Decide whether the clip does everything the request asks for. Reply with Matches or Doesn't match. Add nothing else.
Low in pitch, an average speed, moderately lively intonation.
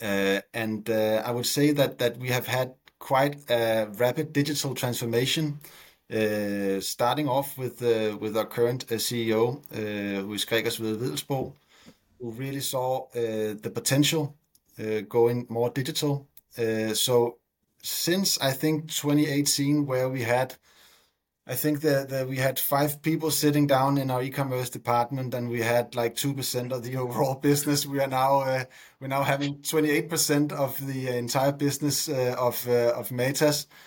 Matches